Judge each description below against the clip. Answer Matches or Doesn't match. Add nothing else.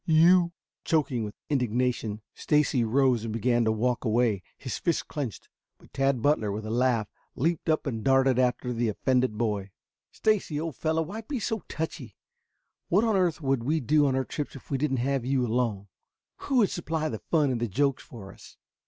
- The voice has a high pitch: Doesn't match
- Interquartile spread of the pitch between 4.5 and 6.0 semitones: Matches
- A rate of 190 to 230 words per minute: Matches